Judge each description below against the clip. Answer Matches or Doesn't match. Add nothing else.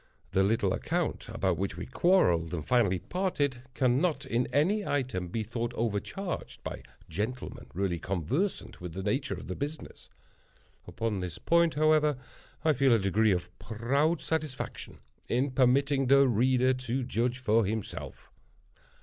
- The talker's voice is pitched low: Matches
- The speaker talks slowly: Doesn't match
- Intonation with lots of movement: Matches